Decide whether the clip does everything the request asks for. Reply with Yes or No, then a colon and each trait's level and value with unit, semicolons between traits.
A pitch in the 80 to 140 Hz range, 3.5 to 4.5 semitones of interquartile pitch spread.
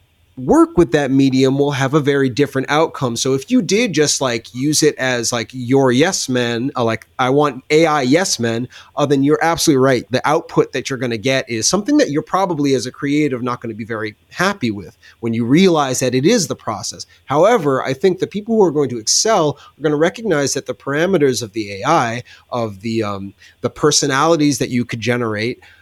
Yes: low, 135 Hz; average, 4.1 semitones